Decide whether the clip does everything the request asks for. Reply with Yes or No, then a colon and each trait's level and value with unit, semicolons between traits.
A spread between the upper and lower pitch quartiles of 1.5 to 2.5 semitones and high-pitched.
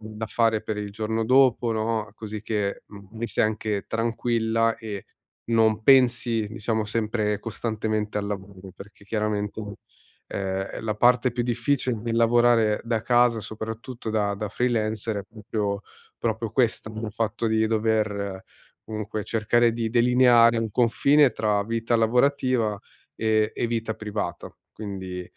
No: narrow, 1.8 semitones; low, 110 Hz